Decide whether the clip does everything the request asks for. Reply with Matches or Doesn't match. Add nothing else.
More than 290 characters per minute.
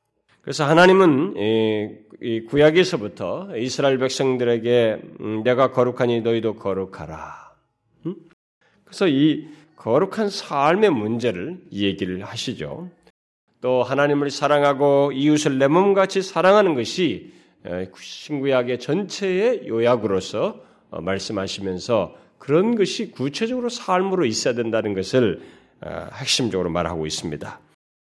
Doesn't match